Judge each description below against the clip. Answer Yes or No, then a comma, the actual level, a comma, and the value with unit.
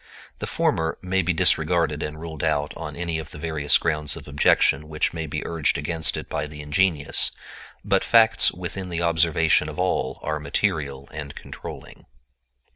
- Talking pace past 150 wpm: Yes, average, 170 wpm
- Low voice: Yes, very low, 80 Hz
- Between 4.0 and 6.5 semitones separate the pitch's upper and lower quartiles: No, narrow, 2.4 semitones